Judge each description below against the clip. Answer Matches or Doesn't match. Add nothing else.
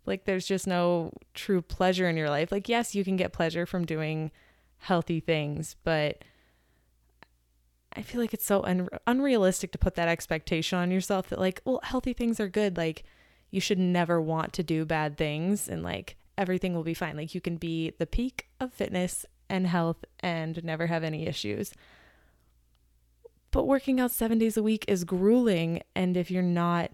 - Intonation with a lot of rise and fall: Doesn't match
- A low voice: Doesn't match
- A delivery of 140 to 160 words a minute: Doesn't match